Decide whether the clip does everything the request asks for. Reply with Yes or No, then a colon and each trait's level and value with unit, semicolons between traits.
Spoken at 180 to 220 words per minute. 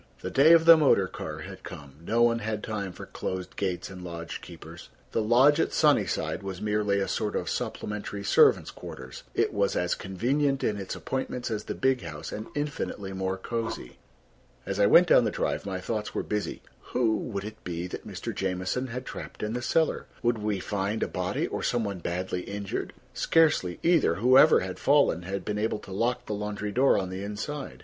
Yes: average, 200 wpm